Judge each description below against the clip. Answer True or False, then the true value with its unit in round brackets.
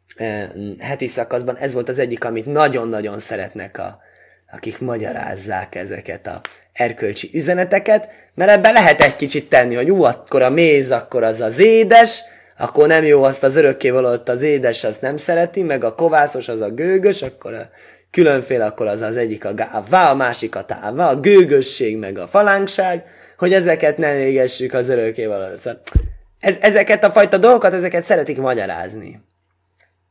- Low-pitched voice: False (145 Hz)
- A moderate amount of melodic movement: False (8.4 semitones)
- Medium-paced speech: False (160 wpm)